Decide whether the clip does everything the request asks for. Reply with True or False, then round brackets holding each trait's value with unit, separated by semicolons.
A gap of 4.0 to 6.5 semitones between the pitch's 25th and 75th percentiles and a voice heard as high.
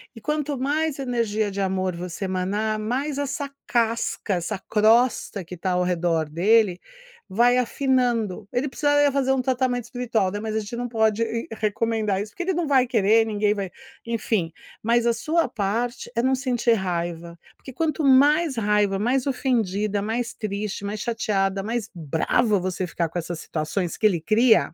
True (4.3 semitones; 220 Hz)